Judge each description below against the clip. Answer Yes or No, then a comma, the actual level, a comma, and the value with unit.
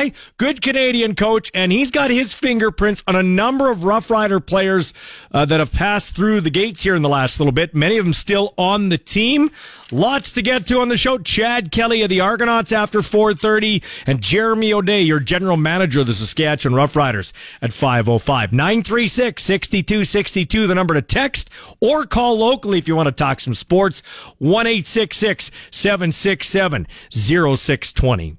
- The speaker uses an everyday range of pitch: No, wide, 6.2 semitones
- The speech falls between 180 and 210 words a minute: No, average, 165 wpm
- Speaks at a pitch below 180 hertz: No, high, 195 Hz